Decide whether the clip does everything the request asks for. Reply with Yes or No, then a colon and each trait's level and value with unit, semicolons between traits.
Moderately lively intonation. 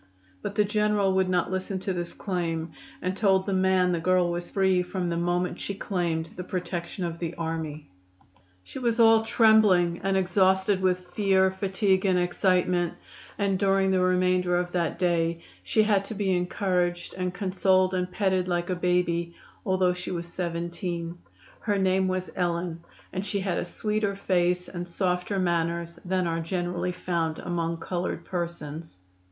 No: narrow, 1.7 semitones